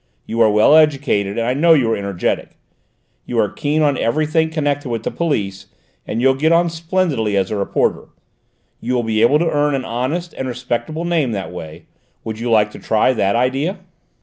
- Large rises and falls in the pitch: Yes, wide, 5.9 semitones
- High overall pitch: No, low, 125 Hz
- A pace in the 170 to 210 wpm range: Yes, average, 200 wpm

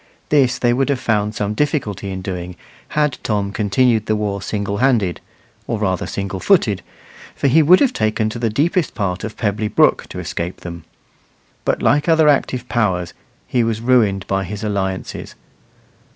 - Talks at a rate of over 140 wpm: Yes, average, 170 wpm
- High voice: No, low, 110 Hz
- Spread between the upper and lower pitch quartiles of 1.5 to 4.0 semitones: No, average, 4.5 semitones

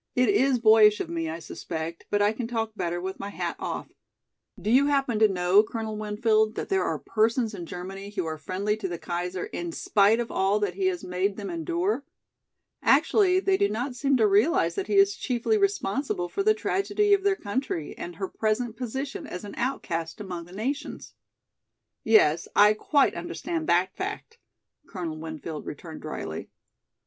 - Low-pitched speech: No, high, 215 Hz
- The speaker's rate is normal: Yes, average, 185 wpm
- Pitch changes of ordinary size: No, wide, 6.9 semitones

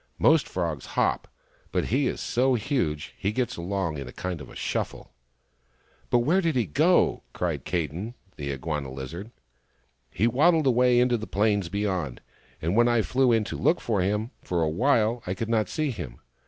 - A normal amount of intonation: No, wide, 6.6 semitones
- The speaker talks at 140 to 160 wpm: No, average, 195 wpm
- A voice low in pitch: Yes, low, 105 Hz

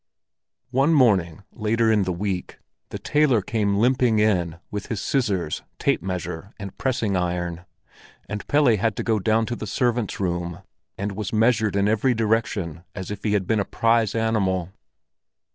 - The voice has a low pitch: Yes, low, 105 Hz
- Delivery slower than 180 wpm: Yes, average, 165 wpm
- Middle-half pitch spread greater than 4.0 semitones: No, average, 3.4 semitones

